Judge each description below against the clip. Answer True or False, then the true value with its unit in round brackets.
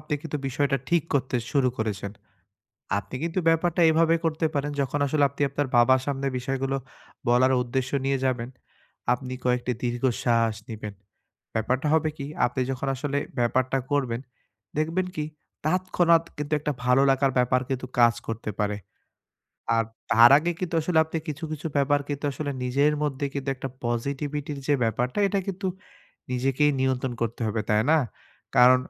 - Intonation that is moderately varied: True (3.4 semitones)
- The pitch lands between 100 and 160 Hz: True (135 Hz)